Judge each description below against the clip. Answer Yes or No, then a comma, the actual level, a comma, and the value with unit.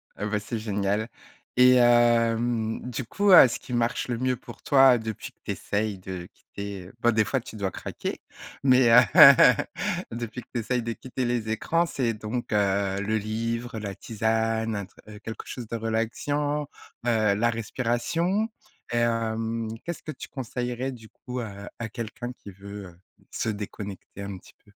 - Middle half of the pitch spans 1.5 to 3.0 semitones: Yes, narrow, 2.6 semitones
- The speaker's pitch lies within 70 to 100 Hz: No, low, 115 Hz